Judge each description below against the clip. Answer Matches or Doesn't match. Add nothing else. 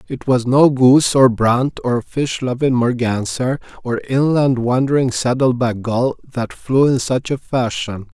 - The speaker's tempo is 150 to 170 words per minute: Matches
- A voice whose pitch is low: Matches